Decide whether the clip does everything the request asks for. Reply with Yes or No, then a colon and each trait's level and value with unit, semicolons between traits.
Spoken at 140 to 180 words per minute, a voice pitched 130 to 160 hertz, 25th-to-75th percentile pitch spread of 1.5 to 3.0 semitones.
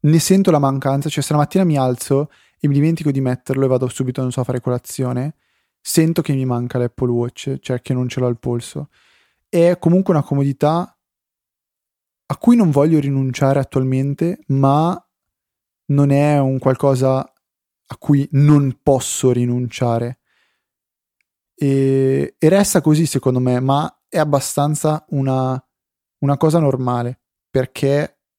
Yes: average, 145 wpm; low, 135 Hz; average, 2.7 semitones